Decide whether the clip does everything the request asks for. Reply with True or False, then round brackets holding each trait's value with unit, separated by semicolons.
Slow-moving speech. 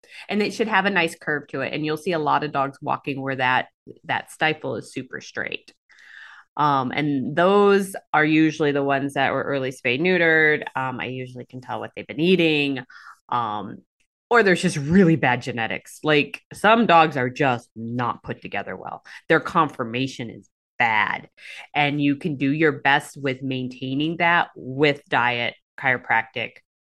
False (170 wpm)